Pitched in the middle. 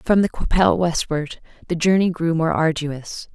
Yes: medium, 170 Hz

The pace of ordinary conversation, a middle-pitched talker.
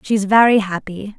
No: average, 150 wpm; high, 205 Hz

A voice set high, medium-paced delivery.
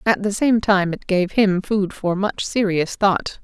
No: high, 195 Hz; fast, 210 wpm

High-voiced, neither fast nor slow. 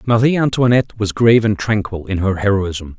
No: low, 105 Hz; average, 180 wpm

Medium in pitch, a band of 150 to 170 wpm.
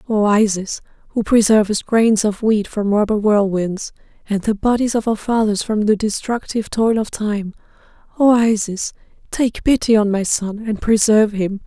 No: high, 215 Hz; average, 165 wpm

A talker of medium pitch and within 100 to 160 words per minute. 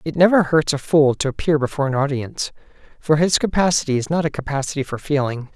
No: medium, 145 Hz; fast, 205 wpm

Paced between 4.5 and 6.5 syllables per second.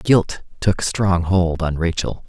No: 3.5 syllables/s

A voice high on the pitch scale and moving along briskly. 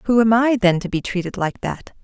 Yes: high, 210 Hz; fast, 265 wpm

